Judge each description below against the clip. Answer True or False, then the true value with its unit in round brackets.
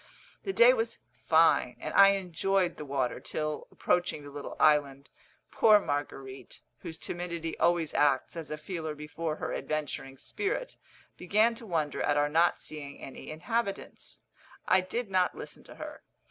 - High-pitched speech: False (160 Hz)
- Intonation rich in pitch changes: False (4.7 semitones)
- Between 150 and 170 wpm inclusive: True (155 wpm)